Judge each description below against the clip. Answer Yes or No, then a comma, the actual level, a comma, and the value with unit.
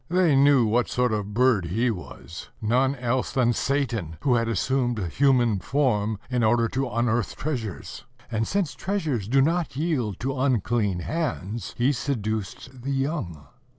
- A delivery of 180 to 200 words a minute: No, average, 155 wpm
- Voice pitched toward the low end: Yes, low, 120 Hz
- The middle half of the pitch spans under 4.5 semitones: Yes, average, 3.9 semitones